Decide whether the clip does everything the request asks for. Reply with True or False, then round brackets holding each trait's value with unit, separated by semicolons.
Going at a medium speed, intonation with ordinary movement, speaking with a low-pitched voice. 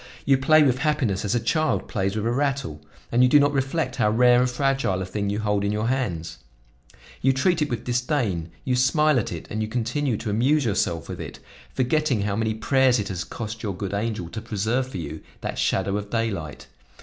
False (220 wpm; 4.7 semitones; 115 Hz)